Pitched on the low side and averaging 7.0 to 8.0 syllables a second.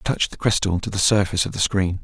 Yes: very low, 95 Hz; 7.4 syllables/s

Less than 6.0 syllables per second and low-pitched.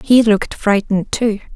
No: 5.3 syllables/s; high, 215 Hz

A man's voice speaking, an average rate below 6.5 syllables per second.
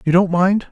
Yes: male; 5.1 syllables/s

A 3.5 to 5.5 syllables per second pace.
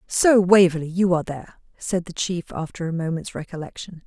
No: 5.7 syllables/s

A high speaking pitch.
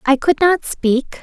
Yes: very high, 290 Hz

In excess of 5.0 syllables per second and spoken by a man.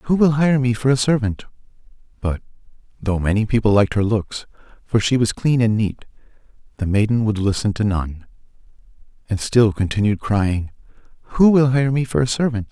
Yes: 5.4 syllables/s; male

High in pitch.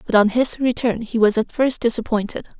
Yes: high, 230 Hz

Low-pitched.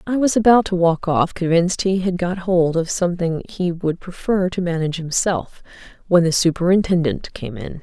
No: medium, 175 Hz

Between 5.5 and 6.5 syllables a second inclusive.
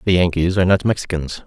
No: 6.8 syllables/s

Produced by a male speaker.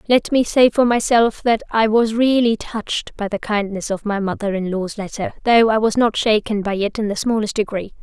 No: female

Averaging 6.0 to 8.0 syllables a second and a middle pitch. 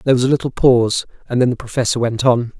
No: 7.2 syllables/s; low, 125 Hz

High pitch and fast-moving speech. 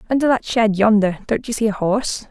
Yes: high, 220 Hz; fast, 235 wpm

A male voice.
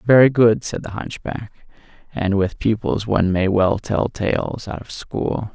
Yes: male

